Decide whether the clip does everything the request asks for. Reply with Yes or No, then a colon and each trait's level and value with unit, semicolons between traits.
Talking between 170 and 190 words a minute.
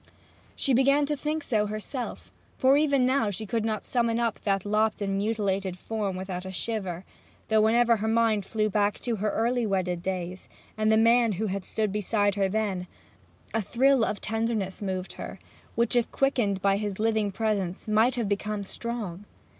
Yes: average, 180 wpm